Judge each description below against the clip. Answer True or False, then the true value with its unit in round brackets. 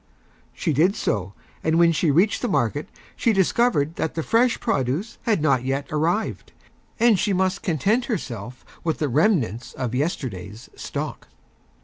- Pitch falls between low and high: True (160 Hz)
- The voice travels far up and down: True (7.4 semitones)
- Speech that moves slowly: False (150 wpm)